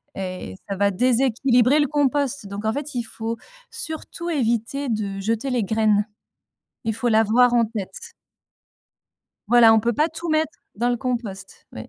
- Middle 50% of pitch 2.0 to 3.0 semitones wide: No, average, 3.9 semitones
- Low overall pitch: No, high, 235 Hz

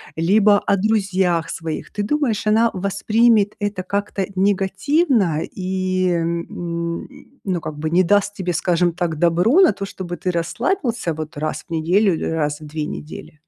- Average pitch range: Yes, average, 3.5 semitones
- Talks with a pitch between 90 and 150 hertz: No, medium, 185 Hz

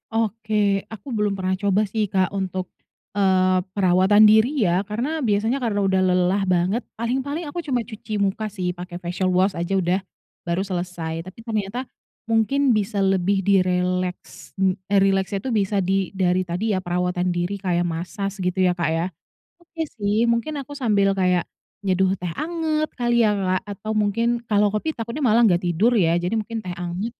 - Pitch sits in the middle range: No, high, 195 Hz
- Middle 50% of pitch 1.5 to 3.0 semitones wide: No, average, 3.4 semitones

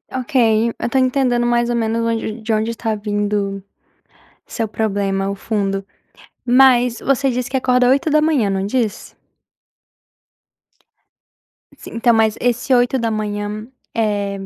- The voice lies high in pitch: Yes, high, 230 Hz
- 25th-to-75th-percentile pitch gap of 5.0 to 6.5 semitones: No, average, 3.2 semitones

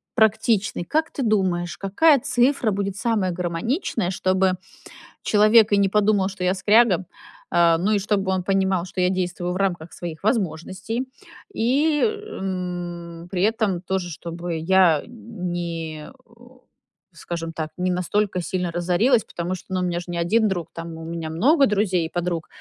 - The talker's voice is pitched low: No, medium, 185 Hz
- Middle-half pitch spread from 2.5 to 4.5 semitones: Yes, average, 3.4 semitones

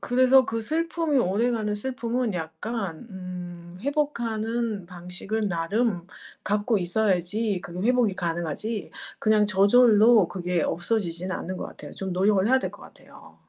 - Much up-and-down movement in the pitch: No, average, 4.6 semitones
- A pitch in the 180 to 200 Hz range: No, high, 210 Hz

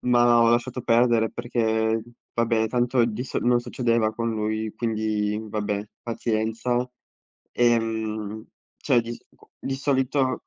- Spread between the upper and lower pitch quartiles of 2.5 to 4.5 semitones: No, narrow, 1.7 semitones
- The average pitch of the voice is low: Yes, low, 115 Hz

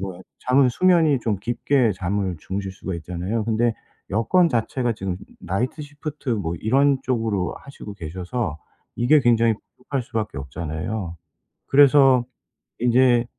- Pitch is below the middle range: Yes, low, 115 Hz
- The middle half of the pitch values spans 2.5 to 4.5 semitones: No, wide, 5.5 semitones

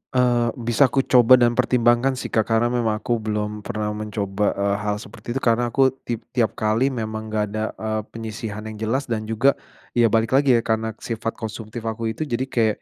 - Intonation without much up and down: Yes, narrow, 1.9 semitones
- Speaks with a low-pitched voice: Yes, low, 115 Hz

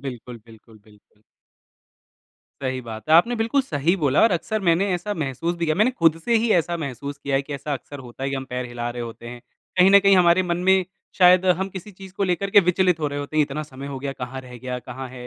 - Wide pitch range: Yes, wide, 6.1 semitones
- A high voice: No, medium, 150 Hz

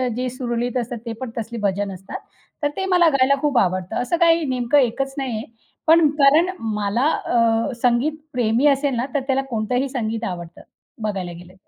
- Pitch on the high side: Yes, high, 245 Hz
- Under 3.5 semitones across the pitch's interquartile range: No, average, 4.2 semitones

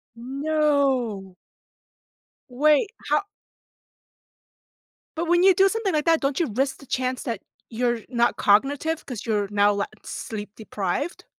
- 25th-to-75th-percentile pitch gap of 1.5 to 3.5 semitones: No, wide, 5.6 semitones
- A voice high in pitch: Yes, very high, 265 Hz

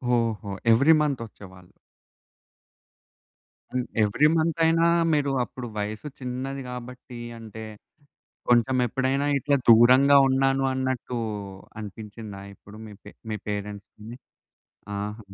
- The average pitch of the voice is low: Yes, low, 120 Hz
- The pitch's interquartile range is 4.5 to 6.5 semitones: No, average, 4.0 semitones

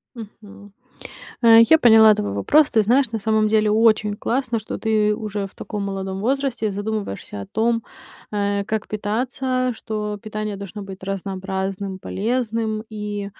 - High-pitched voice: Yes, high, 215 Hz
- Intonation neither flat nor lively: No, narrow, 2.1 semitones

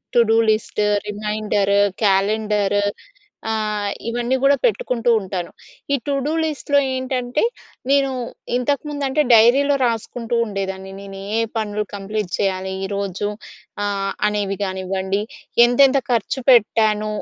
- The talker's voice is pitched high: Yes, high, 215 Hz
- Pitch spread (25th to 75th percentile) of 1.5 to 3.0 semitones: No, average, 3.9 semitones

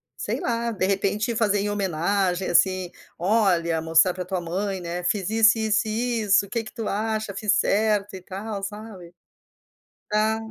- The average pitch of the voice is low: No, high, 200 Hz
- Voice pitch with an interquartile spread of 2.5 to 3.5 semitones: Yes, average, 2.8 semitones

